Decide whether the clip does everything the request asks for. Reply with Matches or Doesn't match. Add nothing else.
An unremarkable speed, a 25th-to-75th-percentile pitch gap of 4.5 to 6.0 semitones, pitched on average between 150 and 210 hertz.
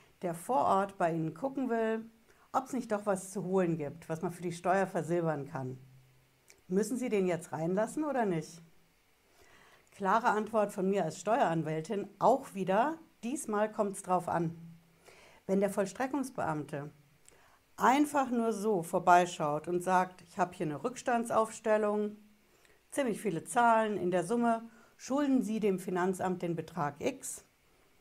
Matches